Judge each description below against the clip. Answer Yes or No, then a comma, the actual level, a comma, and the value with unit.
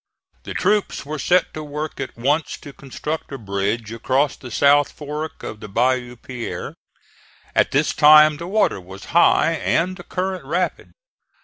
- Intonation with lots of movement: No, average, 4.4 semitones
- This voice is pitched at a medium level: Yes, medium, 145 Hz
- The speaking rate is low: No, average, 165 wpm